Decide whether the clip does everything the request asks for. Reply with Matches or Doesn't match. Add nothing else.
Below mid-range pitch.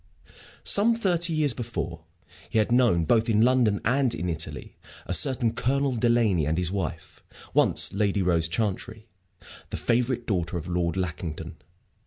Matches